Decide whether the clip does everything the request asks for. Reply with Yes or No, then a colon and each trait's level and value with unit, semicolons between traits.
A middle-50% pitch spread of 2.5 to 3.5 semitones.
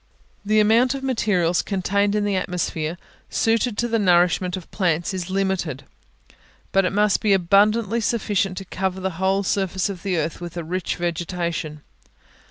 Yes: average, 2.8 semitones